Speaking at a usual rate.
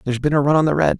No: fast, 425 wpm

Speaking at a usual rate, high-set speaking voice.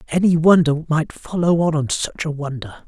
No: average, 165 wpm; medium, 155 Hz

